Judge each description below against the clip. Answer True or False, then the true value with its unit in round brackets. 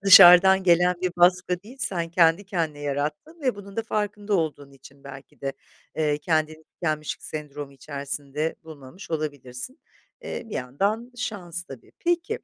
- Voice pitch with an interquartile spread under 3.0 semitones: False (5.2 semitones)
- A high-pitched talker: False (165 Hz)